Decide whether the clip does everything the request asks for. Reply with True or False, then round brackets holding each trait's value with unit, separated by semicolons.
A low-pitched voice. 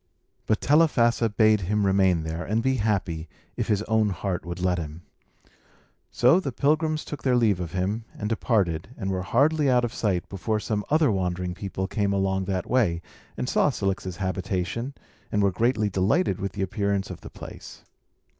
True (100 Hz)